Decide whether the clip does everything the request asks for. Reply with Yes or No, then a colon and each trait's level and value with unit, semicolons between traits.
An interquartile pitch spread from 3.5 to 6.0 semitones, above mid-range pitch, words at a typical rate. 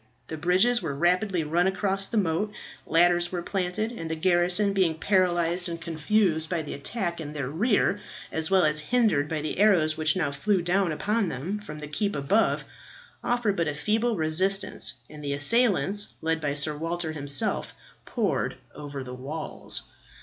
No: average, 4.3 semitones; medium, 175 Hz; average, 170 wpm